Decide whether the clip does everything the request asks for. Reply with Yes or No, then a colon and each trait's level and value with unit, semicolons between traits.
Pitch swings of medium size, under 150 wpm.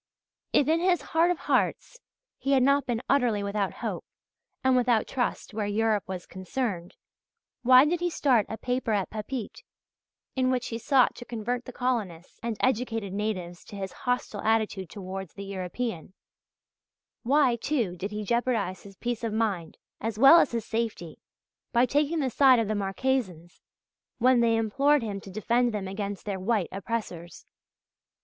No: average, 4.3 semitones; average, 165 wpm